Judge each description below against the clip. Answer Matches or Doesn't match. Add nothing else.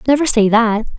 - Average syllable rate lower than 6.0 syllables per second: Matches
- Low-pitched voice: Doesn't match